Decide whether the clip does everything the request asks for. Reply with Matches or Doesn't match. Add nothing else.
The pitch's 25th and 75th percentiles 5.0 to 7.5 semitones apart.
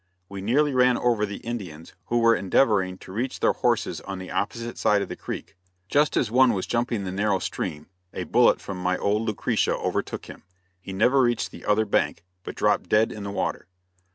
Doesn't match